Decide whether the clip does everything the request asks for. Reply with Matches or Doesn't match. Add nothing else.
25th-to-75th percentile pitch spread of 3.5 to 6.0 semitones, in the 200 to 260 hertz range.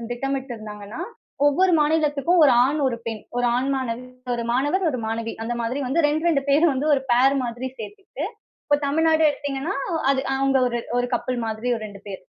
Doesn't match